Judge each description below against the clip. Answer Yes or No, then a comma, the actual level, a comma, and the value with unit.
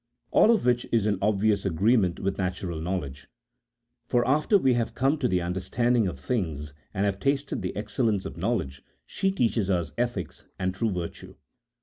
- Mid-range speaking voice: No, low, 100 Hz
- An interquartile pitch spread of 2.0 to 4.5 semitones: No, average, 4.9 semitones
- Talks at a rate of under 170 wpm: No, average, 180 wpm